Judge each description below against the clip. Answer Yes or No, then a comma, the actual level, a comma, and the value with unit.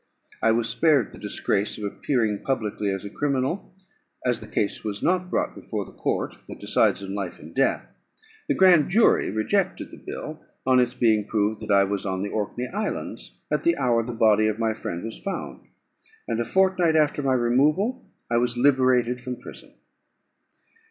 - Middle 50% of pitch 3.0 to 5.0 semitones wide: No, wide, 5.4 semitones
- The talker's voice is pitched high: No, low, 120 Hz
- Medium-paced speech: Yes, average, 185 wpm